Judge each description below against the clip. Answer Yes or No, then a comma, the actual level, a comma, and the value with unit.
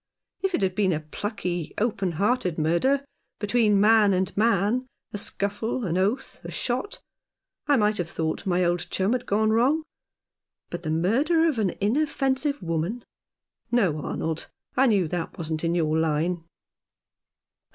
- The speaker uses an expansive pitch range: Yes, wide, 5.9 semitones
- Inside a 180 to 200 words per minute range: No, average, 160 wpm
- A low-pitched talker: No, high, 200 Hz